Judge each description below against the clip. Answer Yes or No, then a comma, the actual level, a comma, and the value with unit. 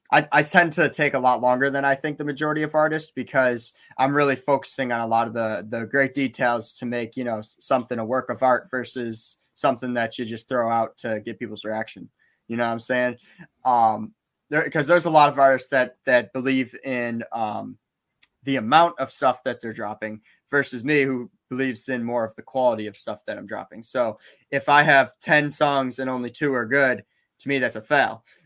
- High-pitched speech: No, low, 130 Hz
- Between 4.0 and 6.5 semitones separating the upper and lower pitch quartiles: No, average, 3.1 semitones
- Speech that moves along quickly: Yes, fast, 215 wpm